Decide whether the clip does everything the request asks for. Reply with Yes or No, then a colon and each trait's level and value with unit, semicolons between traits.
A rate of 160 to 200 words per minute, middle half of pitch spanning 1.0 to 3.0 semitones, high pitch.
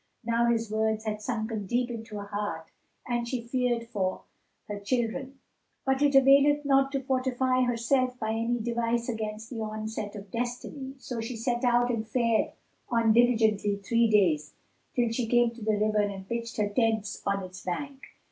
Yes: average, 175 wpm; narrow, 2.5 semitones; high, 230 Hz